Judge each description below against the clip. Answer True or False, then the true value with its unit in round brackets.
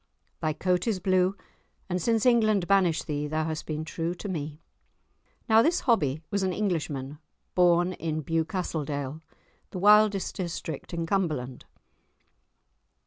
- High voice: False (175 Hz)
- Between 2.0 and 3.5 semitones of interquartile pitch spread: False (4.0 semitones)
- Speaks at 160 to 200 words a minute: False (135 wpm)